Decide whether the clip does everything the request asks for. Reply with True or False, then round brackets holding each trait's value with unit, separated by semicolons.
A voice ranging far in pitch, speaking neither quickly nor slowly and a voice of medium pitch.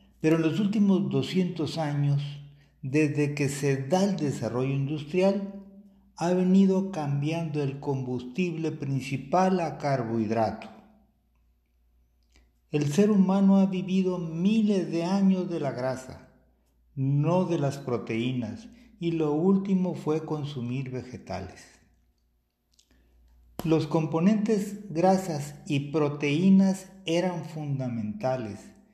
False (6.2 semitones; 100 wpm; 155 Hz)